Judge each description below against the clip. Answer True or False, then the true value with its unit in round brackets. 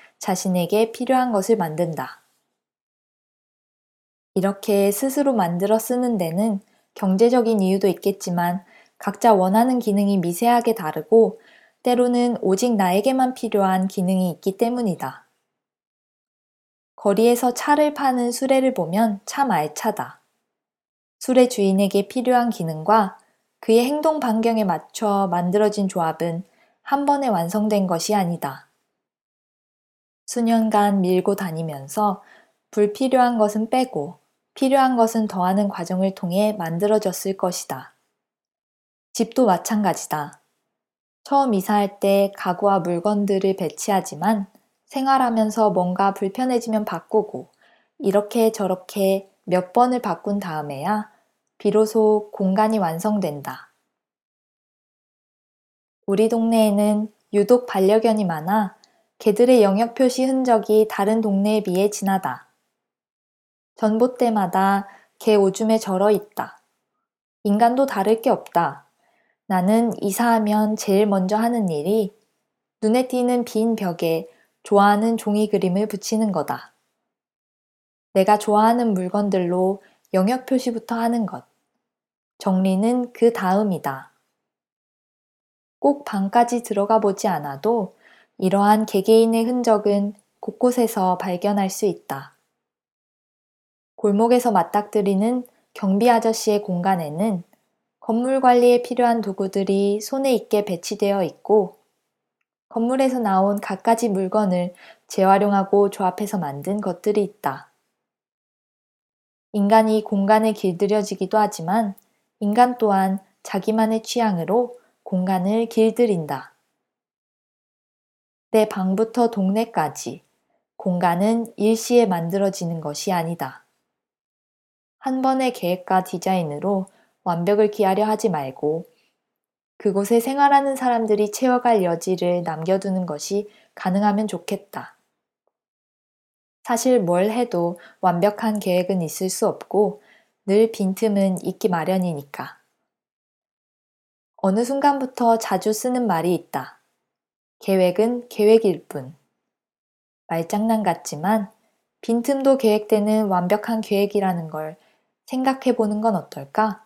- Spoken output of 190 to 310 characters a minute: True (245 characters per minute)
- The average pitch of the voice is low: False (210 Hz)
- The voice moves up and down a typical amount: True (3.1 semitones)